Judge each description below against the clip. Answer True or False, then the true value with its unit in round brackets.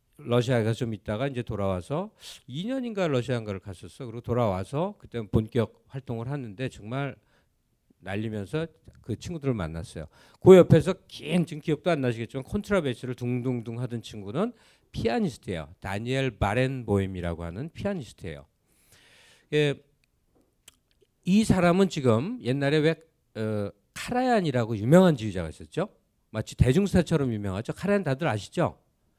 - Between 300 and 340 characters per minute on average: True (335 characters per minute)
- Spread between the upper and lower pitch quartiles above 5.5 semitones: True (6.7 semitones)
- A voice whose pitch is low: True (125 Hz)